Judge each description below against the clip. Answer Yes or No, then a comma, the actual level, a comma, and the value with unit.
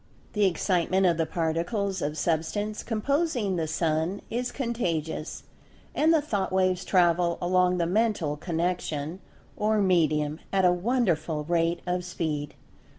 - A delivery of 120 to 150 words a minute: Yes, slow, 135 wpm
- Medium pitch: Yes, medium, 180 Hz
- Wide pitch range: No, average, 4.0 semitones